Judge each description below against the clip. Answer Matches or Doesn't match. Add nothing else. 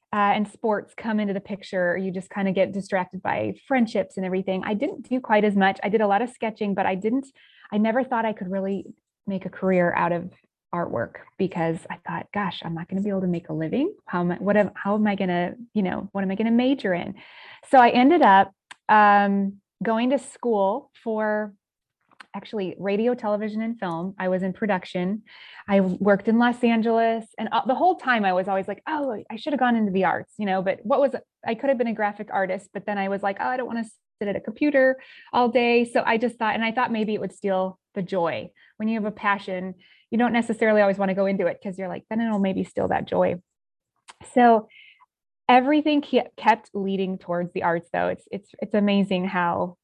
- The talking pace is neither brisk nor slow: Doesn't match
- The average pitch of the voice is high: Matches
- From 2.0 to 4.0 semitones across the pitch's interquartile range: Matches